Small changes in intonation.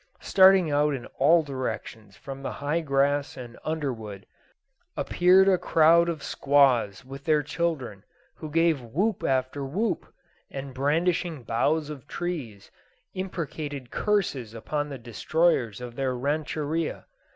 No: average, 4.2 semitones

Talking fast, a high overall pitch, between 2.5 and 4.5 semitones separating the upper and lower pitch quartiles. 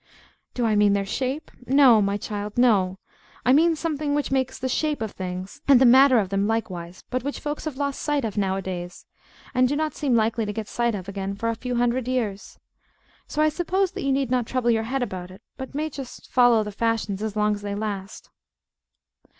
No: fast, 215 wpm; high, 235 Hz; average, 5.0 semitones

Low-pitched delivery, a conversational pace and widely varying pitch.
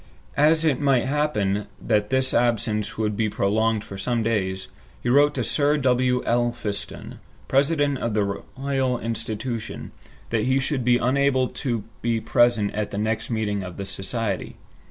No: low, 120 Hz; average, 155 wpm; average, 3.7 semitones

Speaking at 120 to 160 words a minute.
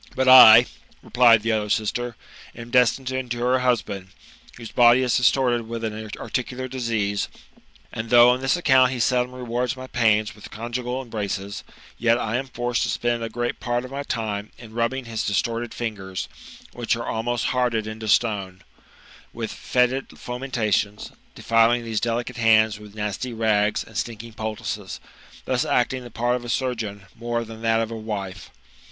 No: average, 175 wpm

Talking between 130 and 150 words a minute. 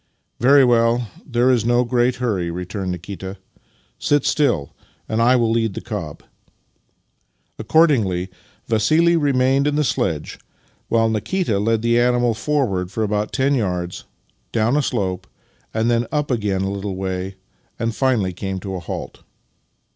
Yes: average, 145 wpm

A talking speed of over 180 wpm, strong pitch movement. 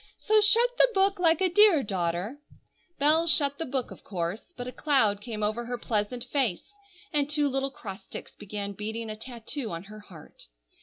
Yes: average, 190 wpm; wide, 6.2 semitones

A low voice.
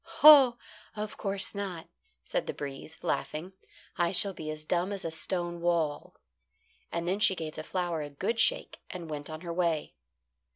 No: medium, 175 Hz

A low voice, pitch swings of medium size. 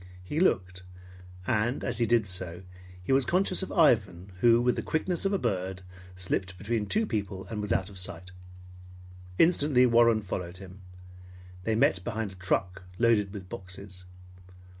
Yes: low, 100 Hz; average, 4.4 semitones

